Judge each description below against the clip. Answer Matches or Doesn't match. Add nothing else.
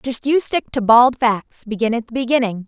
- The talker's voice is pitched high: Matches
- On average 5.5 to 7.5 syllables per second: Doesn't match